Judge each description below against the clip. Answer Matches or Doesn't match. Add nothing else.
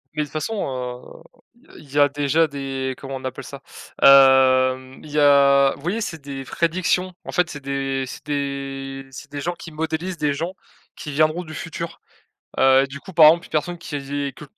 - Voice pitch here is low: Doesn't match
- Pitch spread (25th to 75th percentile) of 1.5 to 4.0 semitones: Matches